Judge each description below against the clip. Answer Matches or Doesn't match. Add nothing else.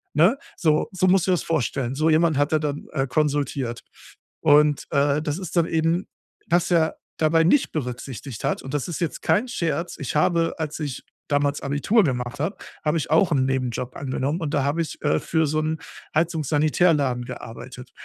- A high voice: Doesn't match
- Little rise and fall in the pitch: Doesn't match